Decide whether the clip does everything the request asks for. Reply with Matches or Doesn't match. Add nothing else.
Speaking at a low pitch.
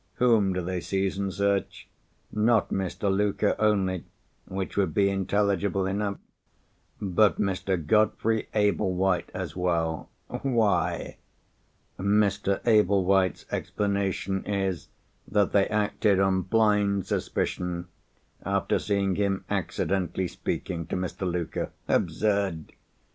Matches